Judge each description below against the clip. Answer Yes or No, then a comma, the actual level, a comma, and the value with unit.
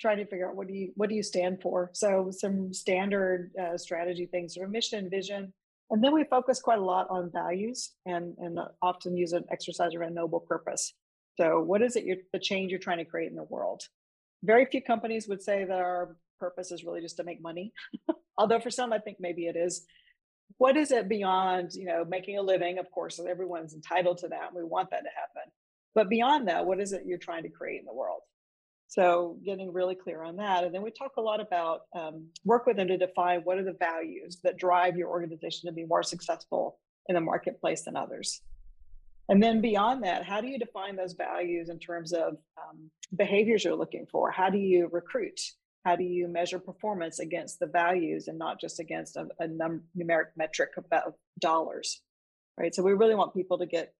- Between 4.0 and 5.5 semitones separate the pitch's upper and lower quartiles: No, average, 3.0 semitones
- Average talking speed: No, fast, 220 wpm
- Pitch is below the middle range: No, medium, 180 Hz